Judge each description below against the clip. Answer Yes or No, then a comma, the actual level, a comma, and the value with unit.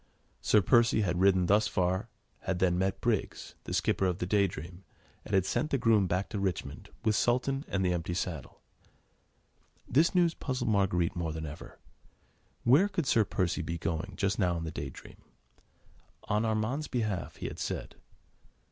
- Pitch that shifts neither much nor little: Yes, average, 4.2 semitones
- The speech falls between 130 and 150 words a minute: No, average, 175 wpm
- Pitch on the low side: Yes, very low, 95 Hz